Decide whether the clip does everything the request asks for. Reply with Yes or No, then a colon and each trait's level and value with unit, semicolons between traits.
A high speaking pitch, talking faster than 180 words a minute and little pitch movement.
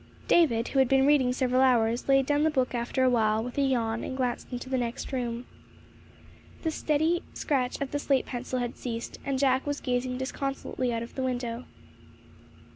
Yes: very high, 255 Hz; average, 195 wpm; narrow, 2.1 semitones